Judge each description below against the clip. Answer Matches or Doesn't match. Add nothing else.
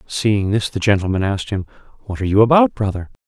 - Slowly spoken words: Doesn't match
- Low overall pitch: Matches